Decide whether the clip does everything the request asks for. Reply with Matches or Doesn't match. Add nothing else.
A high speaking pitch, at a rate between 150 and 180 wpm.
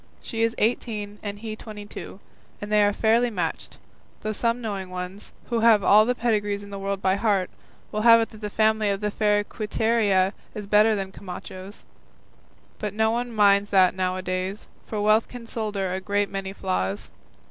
Doesn't match